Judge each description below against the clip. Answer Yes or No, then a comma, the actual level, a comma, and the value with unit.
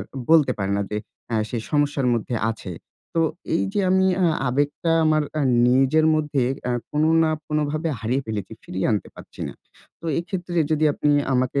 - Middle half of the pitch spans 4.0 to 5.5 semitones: Yes, average, 4.3 semitones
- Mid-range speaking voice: Yes, medium, 145 Hz